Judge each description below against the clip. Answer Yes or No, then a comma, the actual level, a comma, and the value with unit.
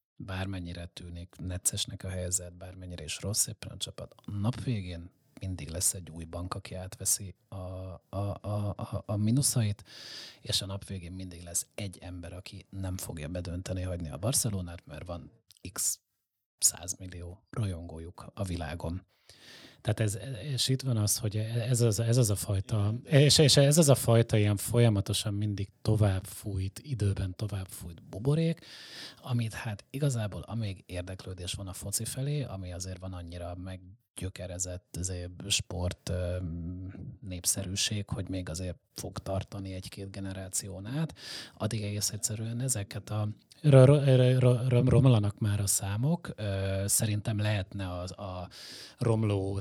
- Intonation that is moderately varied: Yes, average, 3.7 semitones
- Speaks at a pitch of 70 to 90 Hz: No, low, 100 Hz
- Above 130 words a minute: Yes, average, 150 wpm